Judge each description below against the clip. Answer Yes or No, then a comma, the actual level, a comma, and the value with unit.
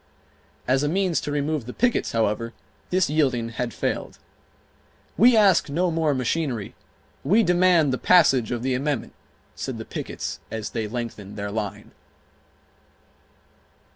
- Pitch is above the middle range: No, low, 135 Hz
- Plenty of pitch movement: Yes, wide, 6.4 semitones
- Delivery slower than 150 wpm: Yes, average, 140 wpm